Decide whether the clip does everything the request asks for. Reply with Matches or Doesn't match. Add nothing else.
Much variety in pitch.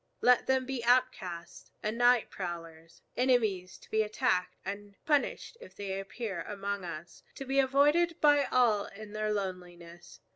Matches